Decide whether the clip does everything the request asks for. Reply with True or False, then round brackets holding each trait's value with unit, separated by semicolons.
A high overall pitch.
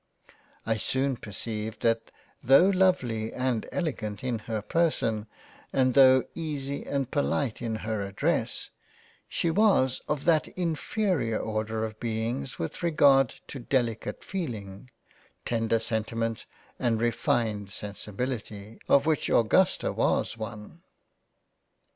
False (120 Hz)